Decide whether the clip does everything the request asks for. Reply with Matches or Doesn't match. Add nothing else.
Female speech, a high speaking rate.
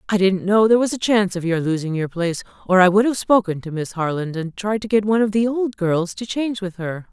Matches